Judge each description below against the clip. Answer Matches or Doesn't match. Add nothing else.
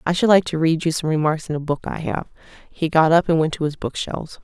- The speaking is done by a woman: Matches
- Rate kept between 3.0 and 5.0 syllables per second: Doesn't match